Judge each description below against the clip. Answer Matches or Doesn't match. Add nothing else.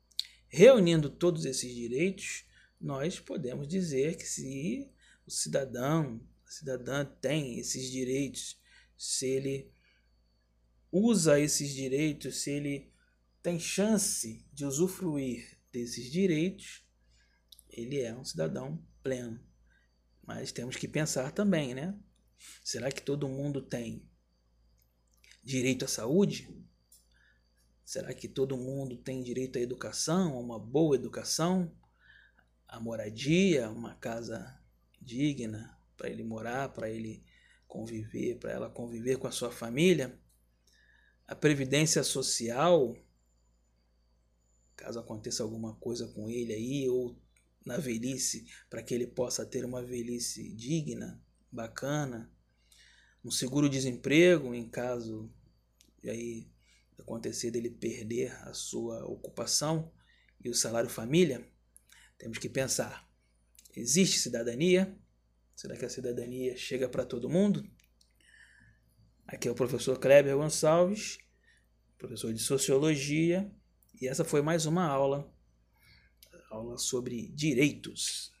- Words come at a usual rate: Doesn't match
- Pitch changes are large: Doesn't match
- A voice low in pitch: Matches